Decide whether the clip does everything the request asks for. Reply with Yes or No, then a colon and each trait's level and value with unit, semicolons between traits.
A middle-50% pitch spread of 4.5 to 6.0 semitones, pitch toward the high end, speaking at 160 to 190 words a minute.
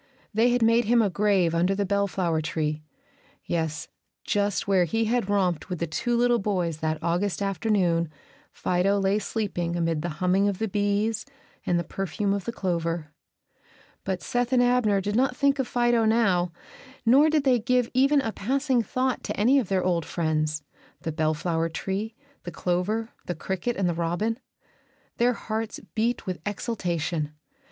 Yes: average, 5.0 semitones; high, 200 Hz; average, 170 wpm